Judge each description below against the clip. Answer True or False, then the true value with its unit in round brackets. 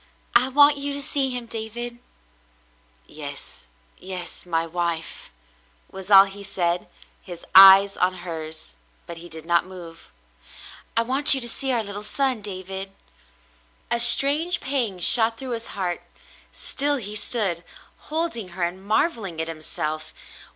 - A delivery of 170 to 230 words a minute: False (145 wpm)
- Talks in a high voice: True (195 Hz)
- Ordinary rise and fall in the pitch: False (5.9 semitones)